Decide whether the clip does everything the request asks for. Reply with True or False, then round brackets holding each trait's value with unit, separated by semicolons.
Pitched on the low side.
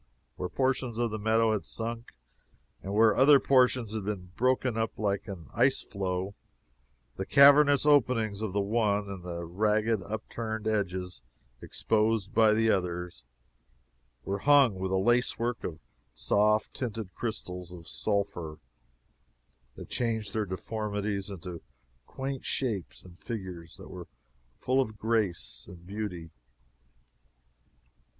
True (105 Hz)